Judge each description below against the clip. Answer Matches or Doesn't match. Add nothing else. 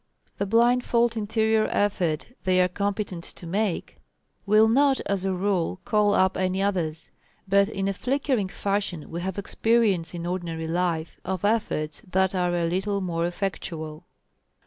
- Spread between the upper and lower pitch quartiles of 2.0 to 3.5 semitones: Matches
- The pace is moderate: Matches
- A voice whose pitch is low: Doesn't match